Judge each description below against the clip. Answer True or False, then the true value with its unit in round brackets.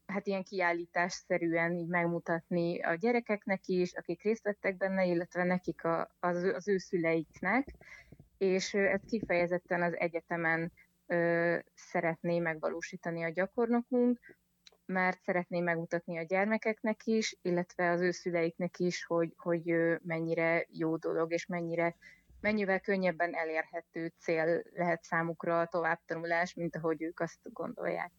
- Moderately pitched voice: True (175 Hz)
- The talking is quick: False (125 wpm)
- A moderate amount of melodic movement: False (2.0 semitones)